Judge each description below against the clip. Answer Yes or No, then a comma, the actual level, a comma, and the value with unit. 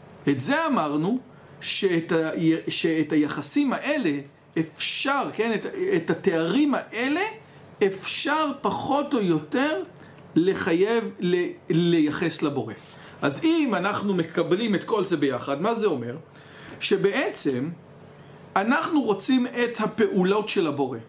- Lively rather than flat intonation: Yes, wide, 8.8 semitones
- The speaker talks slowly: Yes, slow, 115 wpm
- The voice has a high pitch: Yes, high, 195 Hz